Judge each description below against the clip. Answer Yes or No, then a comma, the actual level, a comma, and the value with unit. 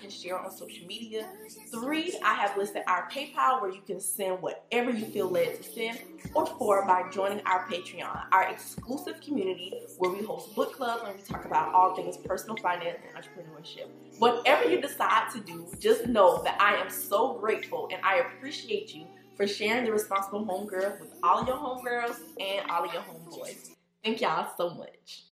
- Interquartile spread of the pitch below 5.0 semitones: No, wide, 5.5 semitones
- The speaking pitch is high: Yes, high, 220 Hz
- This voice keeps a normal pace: Yes, average, 185 wpm